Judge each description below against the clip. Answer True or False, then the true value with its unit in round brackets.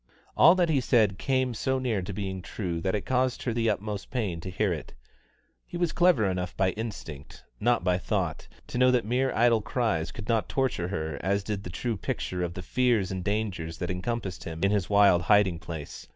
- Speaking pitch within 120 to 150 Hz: False (100 Hz)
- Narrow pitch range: False (4.9 semitones)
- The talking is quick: True (210 wpm)